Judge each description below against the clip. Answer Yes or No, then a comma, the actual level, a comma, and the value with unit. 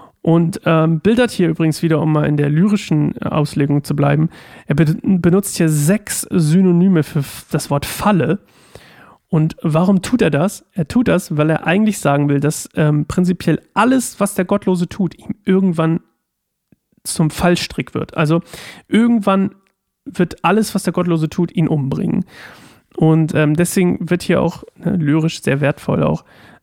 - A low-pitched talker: No, medium, 170 Hz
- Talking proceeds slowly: No, average, 160 wpm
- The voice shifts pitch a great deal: No, average, 3.7 semitones